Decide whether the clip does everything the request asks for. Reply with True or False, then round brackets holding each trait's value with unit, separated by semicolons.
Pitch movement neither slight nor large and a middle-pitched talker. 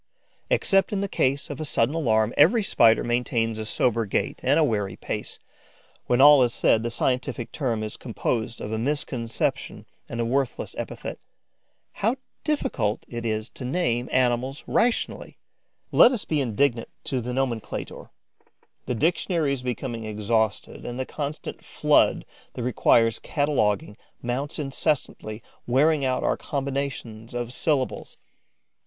False (3.9 semitones; 125 Hz)